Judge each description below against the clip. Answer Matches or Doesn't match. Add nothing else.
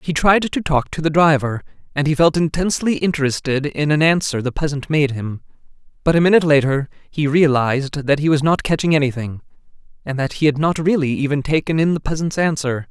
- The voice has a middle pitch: Matches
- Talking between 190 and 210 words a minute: Matches